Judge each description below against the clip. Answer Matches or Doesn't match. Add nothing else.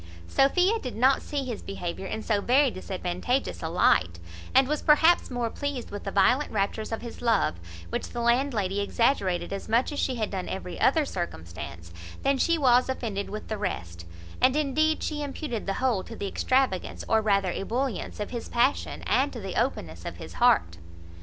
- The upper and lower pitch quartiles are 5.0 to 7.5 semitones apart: Matches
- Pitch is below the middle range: Doesn't match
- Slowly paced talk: Doesn't match